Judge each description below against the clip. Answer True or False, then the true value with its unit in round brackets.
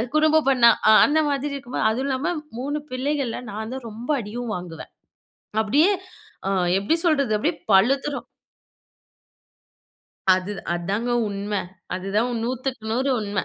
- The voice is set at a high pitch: True (245 Hz)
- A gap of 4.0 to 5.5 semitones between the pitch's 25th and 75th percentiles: True (4.9 semitones)